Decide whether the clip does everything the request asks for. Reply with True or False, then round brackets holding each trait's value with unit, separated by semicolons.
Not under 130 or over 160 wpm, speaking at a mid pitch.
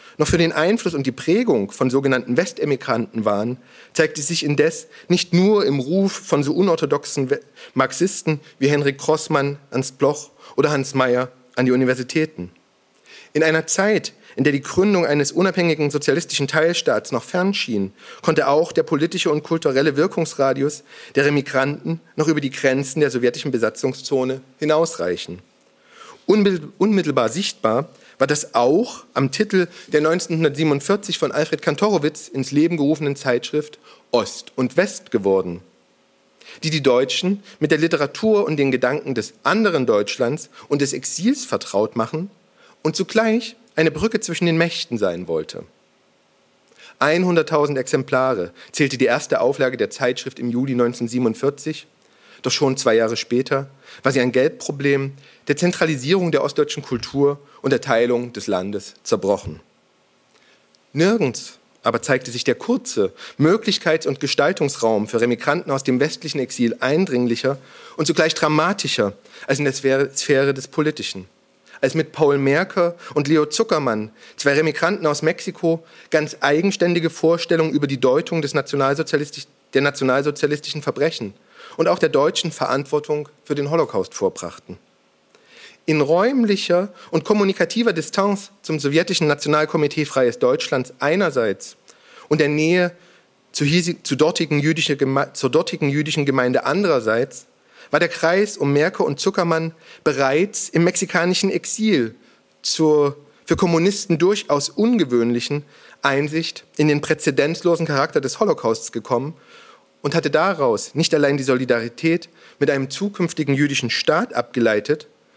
True (135 wpm; 150 Hz)